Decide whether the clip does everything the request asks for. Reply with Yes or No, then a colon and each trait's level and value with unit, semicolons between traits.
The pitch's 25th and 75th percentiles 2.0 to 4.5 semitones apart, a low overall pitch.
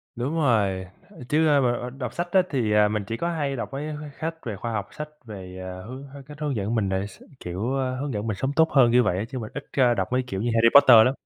No: average, 5.2 semitones; low, 120 Hz